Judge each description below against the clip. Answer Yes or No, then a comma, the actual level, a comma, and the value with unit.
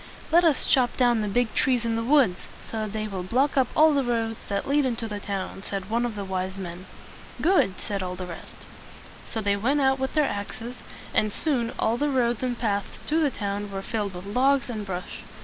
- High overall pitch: Yes, high, 225 Hz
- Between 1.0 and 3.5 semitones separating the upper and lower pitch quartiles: No, average, 4.6 semitones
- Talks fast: Yes, fast, 225 wpm